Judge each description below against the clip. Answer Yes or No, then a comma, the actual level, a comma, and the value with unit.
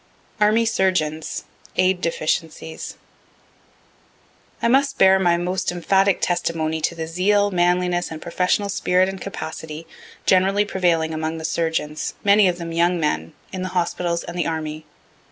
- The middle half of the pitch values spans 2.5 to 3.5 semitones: Yes, average, 2.8 semitones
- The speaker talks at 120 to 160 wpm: Yes, average, 140 wpm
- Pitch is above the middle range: No, medium, 175 Hz